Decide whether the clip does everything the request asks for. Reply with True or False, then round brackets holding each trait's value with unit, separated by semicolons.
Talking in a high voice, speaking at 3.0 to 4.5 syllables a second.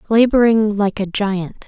True (210 Hz; 4.0 syllables/s)